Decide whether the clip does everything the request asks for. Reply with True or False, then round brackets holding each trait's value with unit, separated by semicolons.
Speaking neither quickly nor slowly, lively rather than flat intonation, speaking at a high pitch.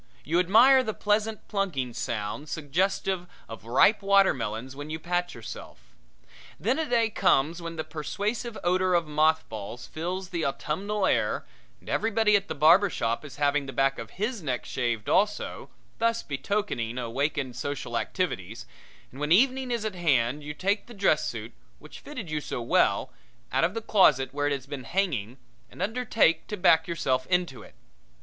False (170 wpm; 7.0 semitones; 165 Hz)